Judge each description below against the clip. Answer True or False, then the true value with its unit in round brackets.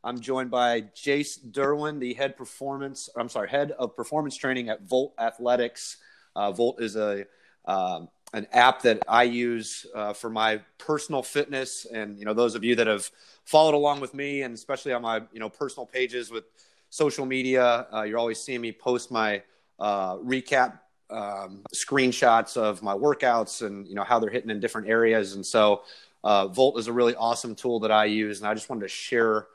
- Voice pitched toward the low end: True (120 Hz)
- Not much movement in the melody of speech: False (3.2 semitones)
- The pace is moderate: True (195 wpm)